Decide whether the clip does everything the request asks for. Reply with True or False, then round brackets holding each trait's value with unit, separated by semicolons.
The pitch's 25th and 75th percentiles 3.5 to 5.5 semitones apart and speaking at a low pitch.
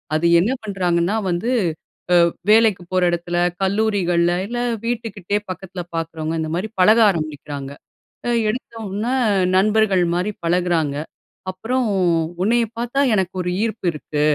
False (4.2 semitones; 185 Hz)